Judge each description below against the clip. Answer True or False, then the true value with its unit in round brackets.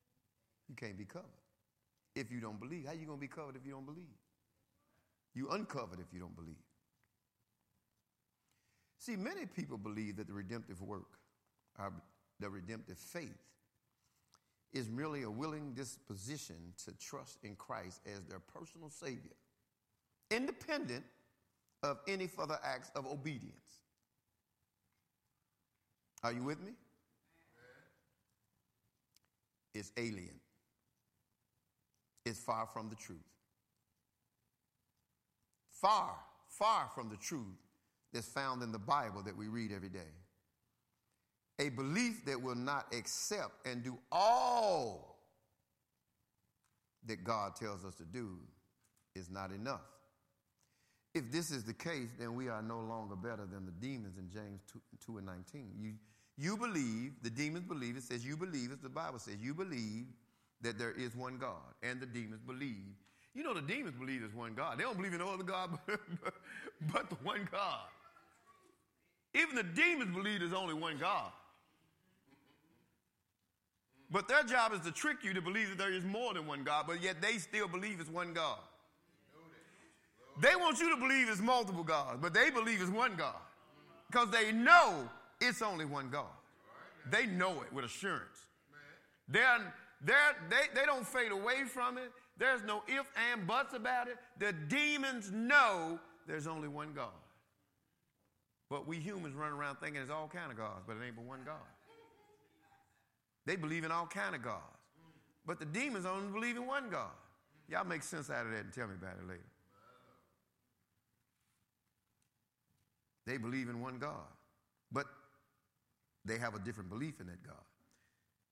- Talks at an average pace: True (155 wpm)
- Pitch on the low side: True (130 Hz)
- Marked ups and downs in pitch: True (8.9 semitones)